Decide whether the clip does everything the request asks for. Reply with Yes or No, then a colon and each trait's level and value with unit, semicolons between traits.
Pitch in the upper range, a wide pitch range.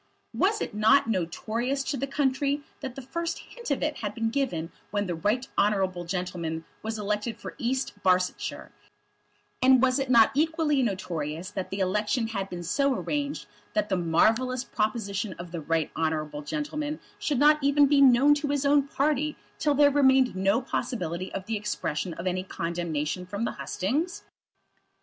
Yes: high, 225 Hz; wide, 7.1 semitones